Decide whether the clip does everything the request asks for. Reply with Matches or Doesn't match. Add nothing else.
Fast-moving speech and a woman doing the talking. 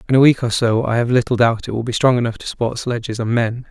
Doesn't match